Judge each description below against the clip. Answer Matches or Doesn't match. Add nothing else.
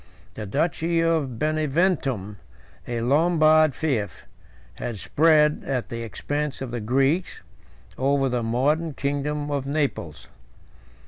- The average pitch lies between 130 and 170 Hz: Matches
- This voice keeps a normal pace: Doesn't match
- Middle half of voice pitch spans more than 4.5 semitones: Doesn't match